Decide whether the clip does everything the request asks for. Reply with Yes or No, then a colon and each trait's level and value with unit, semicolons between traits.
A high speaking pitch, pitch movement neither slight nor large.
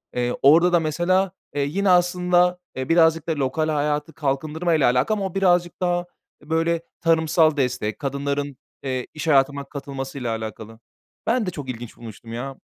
No: medium, 150 Hz; average, 4.4 semitones